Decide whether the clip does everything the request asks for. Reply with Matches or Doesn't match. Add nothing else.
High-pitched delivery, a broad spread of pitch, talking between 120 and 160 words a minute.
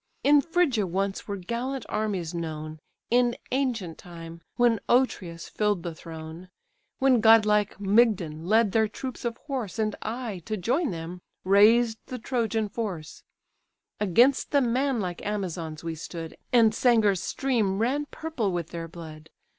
Matches